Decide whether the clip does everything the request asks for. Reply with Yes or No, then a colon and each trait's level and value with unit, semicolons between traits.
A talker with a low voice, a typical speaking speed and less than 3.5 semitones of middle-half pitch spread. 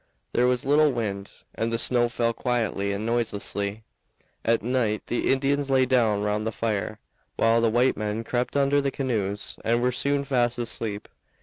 Yes: low, 115 Hz; average, 175 wpm; average, 3.1 semitones